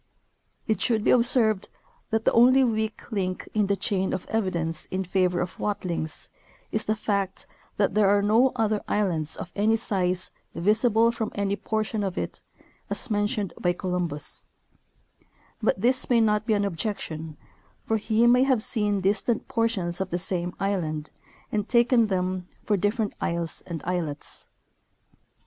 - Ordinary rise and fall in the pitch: Yes, average, 3.4 semitones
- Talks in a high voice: Yes, high, 205 Hz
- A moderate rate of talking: Yes, average, 155 wpm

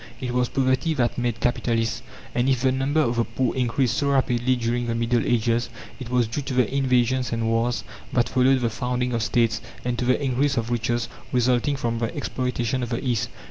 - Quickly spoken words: Yes, fast, 210 wpm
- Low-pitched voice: Yes, low, 125 Hz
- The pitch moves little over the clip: Yes, narrow, 1.7 semitones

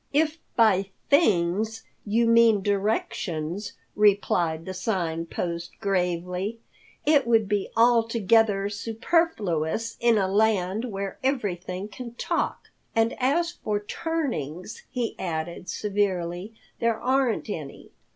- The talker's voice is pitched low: No, high, 205 Hz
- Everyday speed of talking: No, slow, 110 wpm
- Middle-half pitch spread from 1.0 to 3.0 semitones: No, average, 4.2 semitones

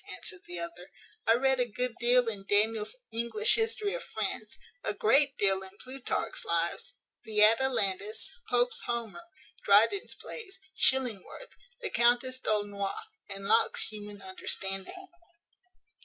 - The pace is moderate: No, slow, 125 wpm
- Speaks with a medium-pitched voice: No, high, 230 Hz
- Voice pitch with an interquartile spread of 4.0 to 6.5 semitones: Yes, average, 4.7 semitones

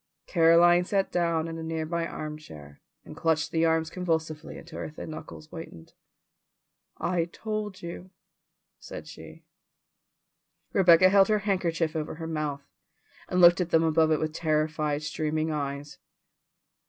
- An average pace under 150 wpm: Yes, average, 140 wpm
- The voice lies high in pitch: No, medium, 165 Hz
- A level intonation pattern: Yes, narrow, 2.0 semitones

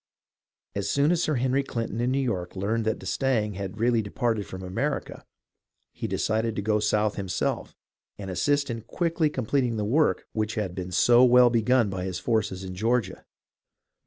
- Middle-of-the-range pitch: No, low, 110 Hz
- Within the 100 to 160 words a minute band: No, average, 175 wpm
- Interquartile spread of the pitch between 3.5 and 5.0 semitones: Yes, average, 3.9 semitones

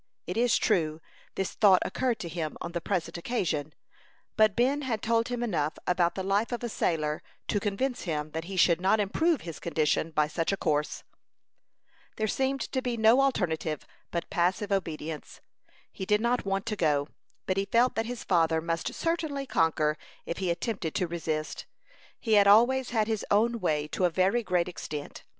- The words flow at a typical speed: Yes, average, 185 wpm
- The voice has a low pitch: No, high, 190 Hz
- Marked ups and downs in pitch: Yes, wide, 6.0 semitones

